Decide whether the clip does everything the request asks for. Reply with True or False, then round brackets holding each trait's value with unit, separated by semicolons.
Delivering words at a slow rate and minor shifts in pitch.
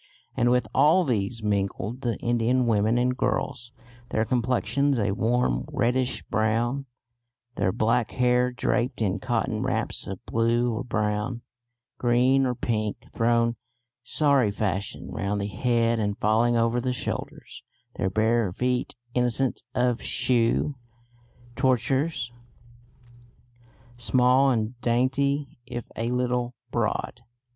True (120 wpm; 2.2 semitones)